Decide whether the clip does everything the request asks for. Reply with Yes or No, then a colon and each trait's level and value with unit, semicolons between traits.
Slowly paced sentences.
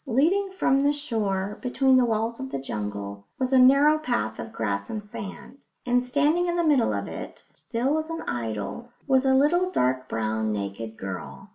No: average, 185 wpm